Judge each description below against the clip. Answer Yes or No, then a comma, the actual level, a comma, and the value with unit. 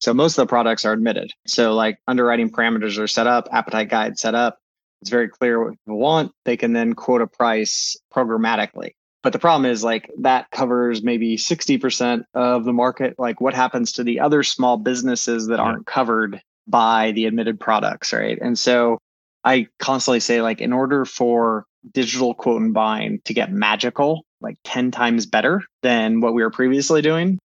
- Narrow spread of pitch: Yes, narrow, 1.9 semitones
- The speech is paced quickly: No, average, 185 wpm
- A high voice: No, low, 120 Hz